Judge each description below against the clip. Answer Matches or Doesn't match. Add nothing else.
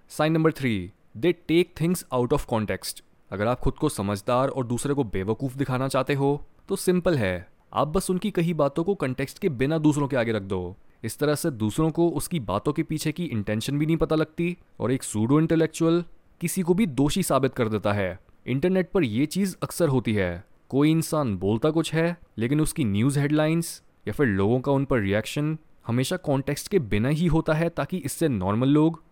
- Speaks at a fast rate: Matches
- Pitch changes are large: Matches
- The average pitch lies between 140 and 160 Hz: Matches